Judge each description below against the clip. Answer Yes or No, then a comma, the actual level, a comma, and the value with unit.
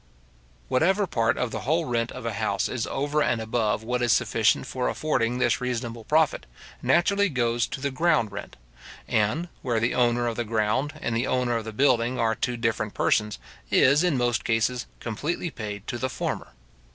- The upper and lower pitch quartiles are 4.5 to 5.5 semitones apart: No, average, 3.3 semitones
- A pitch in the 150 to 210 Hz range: No, low, 120 Hz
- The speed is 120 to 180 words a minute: No, average, 190 wpm